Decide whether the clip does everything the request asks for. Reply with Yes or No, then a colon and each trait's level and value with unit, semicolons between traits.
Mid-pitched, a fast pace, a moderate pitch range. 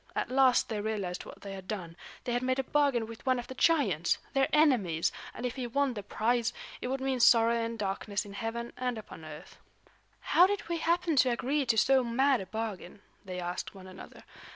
No: high, 235 Hz; fast, 215 wpm; average, 4.5 semitones